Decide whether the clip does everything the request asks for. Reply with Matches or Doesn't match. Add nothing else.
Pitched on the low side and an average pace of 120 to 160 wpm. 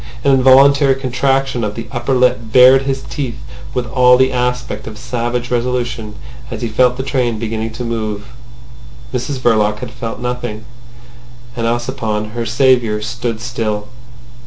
Matches